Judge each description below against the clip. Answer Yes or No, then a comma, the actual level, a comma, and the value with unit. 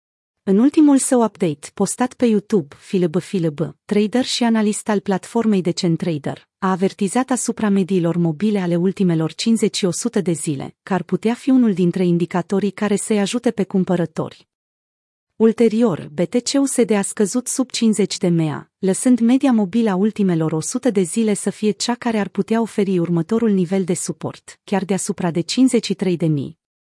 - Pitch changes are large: No, average, 4.3 semitones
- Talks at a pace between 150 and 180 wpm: Yes, average, 155 wpm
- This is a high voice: Yes, high, 200 Hz